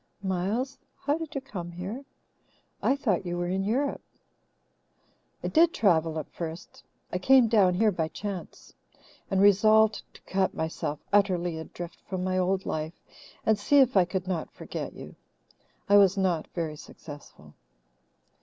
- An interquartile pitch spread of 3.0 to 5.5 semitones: Yes, average, 3.8 semitones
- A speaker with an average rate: Yes, average, 155 wpm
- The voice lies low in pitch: No, high, 190 Hz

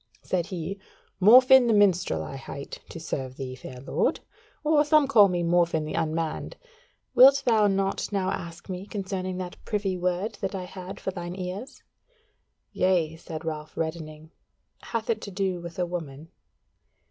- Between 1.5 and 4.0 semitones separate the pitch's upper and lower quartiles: Yes, average, 3.7 semitones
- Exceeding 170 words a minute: No, average, 160 wpm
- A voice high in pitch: No, medium, 180 Hz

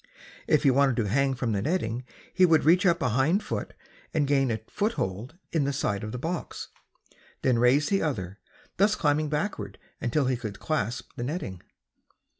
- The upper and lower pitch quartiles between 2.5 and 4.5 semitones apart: No, average, 5.3 semitones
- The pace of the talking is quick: No, average, 185 wpm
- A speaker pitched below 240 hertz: Yes, low, 135 Hz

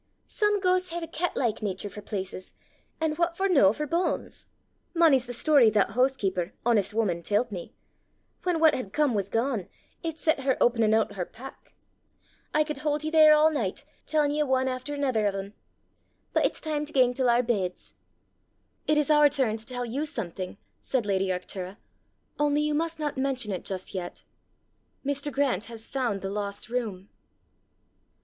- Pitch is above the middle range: Yes, very high, 255 Hz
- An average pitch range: No, wide, 6.6 semitones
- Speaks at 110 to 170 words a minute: No, average, 185 wpm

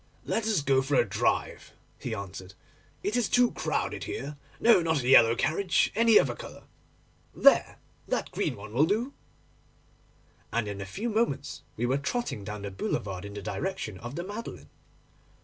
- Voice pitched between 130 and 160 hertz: Yes, medium, 140 Hz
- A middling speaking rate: Yes, average, 170 wpm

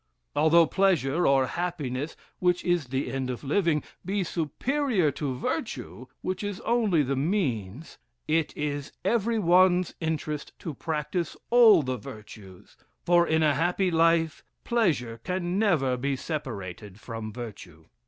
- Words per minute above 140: No, slow, 135 wpm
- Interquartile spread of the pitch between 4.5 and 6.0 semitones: Yes, wide, 5.5 semitones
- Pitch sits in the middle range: Yes, medium, 160 Hz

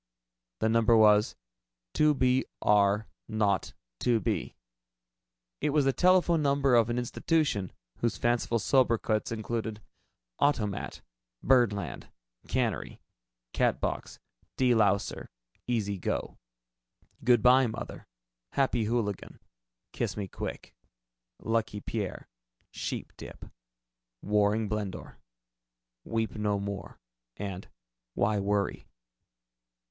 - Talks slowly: Yes, slow, 95 wpm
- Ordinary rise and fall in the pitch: Yes, average, 3.1 semitones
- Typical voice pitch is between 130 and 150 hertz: No, low, 110 Hz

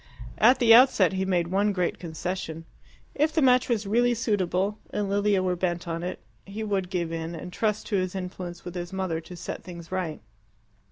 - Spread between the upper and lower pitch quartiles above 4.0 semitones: No, average, 3.2 semitones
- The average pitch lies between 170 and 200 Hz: Yes, medium, 185 Hz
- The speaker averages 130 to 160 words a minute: No, average, 200 wpm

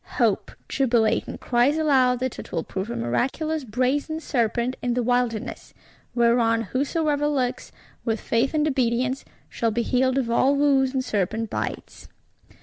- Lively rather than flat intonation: No, average, 2.9 semitones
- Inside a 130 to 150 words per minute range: Yes, average, 145 wpm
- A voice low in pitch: No, very high, 250 Hz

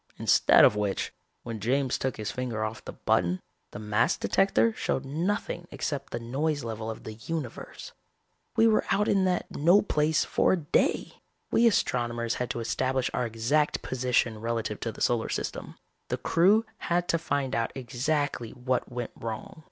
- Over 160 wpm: Yes, average, 170 wpm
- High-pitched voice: No, low, 125 Hz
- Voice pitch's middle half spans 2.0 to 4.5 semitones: No, wide, 5.5 semitones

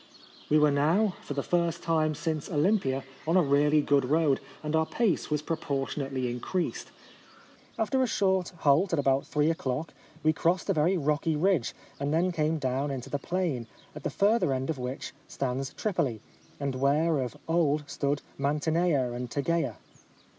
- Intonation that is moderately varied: Yes, average, 3.4 semitones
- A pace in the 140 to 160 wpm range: No, average, 170 wpm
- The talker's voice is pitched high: No, medium, 150 Hz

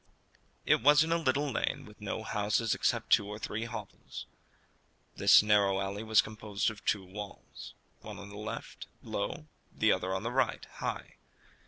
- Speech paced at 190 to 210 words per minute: No, average, 170 wpm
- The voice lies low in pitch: Yes, low, 105 Hz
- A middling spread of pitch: No, narrow, 2.1 semitones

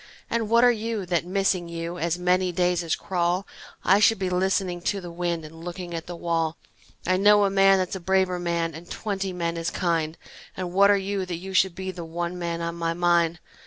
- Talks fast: Yes, fast, 225 wpm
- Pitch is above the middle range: No, medium, 180 Hz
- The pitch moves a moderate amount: No, narrow, 2.1 semitones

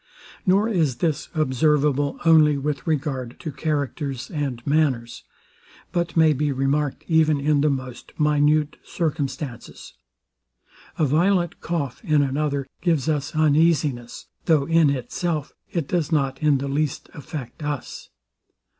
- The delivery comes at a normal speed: No, slow, 130 wpm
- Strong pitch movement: No, narrow, 2.4 semitones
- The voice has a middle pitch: Yes, medium, 150 Hz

